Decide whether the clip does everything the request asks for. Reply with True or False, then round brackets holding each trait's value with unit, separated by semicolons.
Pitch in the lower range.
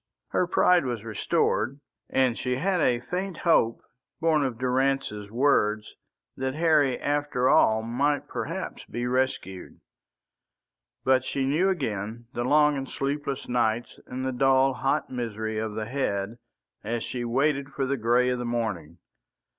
True (130 Hz)